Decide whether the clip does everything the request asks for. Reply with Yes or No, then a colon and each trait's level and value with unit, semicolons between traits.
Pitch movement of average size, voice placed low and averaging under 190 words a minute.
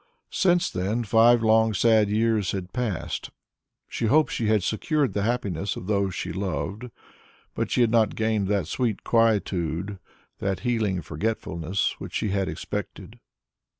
Yes: average, 3.2 semitones; low, 105 Hz; average, 150 wpm